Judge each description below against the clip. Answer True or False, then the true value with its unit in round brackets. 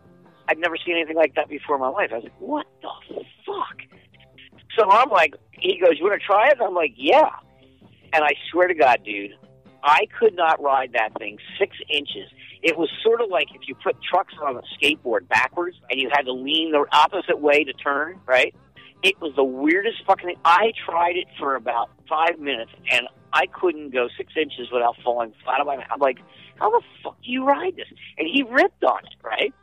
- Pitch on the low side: False (165 Hz)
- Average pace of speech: False (220 wpm)